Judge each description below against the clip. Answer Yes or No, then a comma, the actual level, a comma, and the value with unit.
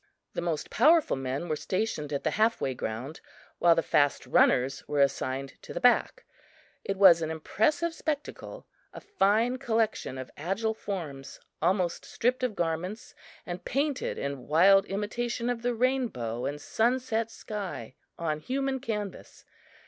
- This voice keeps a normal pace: Yes, average, 150 wpm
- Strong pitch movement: Yes, wide, 8.3 semitones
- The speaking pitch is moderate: No, high, 195 Hz